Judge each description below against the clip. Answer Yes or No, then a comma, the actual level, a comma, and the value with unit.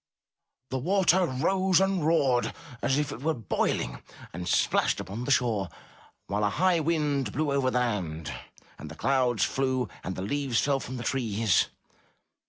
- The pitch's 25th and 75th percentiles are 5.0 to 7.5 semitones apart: Yes, average, 5.3 semitones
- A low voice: Yes, low, 130 Hz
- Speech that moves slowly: No, average, 165 wpm